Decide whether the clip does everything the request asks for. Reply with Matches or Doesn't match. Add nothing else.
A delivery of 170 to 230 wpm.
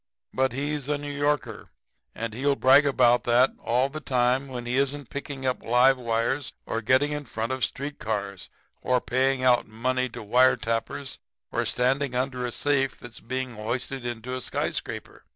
Matches